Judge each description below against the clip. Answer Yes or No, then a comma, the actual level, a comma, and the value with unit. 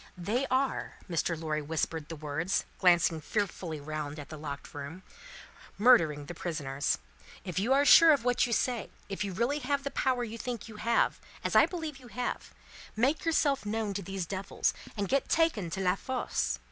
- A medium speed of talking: Yes, average, 185 wpm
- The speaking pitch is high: Yes, high, 200 Hz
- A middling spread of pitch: No, wide, 7.5 semitones